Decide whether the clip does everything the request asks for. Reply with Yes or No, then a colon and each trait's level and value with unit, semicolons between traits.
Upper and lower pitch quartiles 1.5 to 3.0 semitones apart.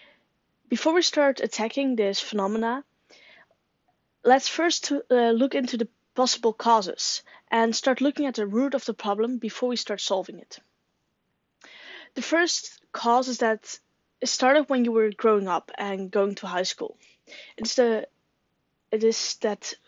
No: average, 3.8 semitones